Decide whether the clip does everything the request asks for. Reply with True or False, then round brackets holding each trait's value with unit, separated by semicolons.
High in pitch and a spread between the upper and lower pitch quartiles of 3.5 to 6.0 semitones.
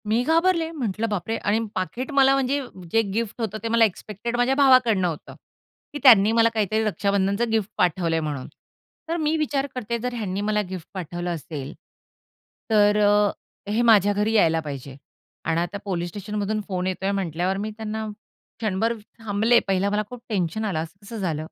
True (210 Hz; 3.9 semitones)